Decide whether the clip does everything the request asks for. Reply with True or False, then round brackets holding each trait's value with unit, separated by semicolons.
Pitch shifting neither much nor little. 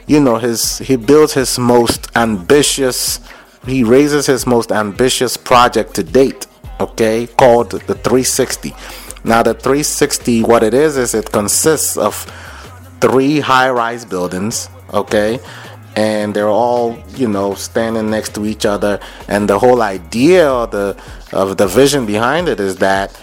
True (3.6 semitones)